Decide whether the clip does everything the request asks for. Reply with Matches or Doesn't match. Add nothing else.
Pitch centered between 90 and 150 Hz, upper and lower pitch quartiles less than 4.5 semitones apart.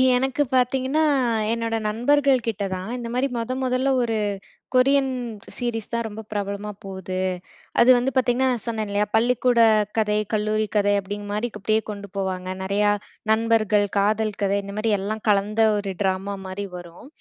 Doesn't match